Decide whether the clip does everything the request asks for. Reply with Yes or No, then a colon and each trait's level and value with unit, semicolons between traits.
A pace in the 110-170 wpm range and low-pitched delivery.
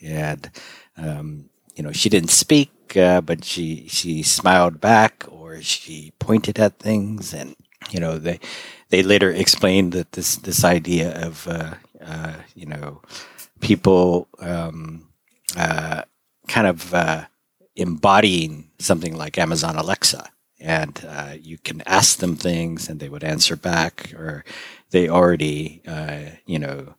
Yes: average, 140 wpm; very low, 85 Hz